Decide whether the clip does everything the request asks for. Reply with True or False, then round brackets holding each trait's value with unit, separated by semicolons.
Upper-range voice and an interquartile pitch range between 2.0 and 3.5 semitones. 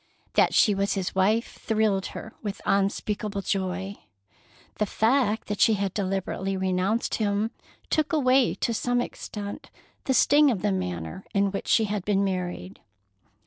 True (200 Hz; 2.6 semitones)